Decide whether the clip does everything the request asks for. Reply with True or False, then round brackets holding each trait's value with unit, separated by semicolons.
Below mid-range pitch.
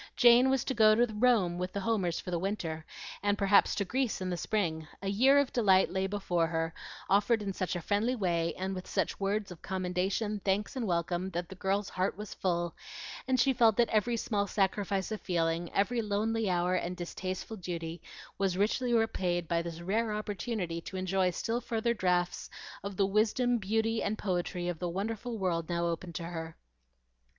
False (195 Hz)